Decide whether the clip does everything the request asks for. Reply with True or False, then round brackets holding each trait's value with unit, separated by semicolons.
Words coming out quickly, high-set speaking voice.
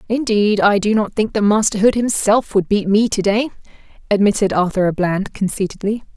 False (185 wpm; 205 Hz)